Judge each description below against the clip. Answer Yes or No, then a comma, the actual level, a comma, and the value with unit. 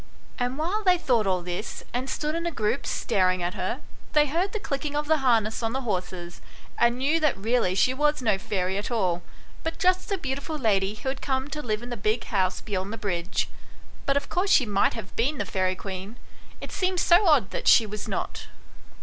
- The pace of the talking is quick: Yes, fast, 220 wpm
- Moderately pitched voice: No, high, 240 Hz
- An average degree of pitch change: No, wide, 7.2 semitones